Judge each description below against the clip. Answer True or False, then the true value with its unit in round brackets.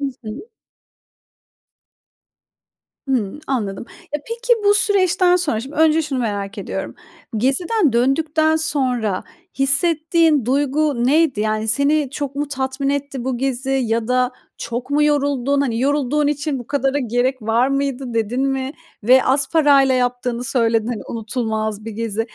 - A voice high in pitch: True (265 Hz)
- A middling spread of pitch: True (3.7 semitones)